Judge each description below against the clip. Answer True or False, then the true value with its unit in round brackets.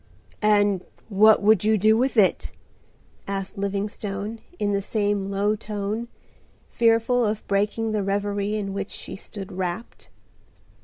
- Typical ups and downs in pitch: False (1.5 semitones)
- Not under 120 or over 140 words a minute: True (135 wpm)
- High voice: True (205 Hz)